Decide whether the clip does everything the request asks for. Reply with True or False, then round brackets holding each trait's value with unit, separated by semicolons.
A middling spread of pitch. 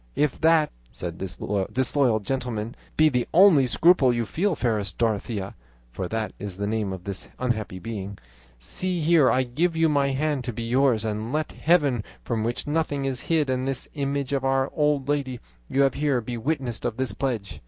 True (4.7 semitones)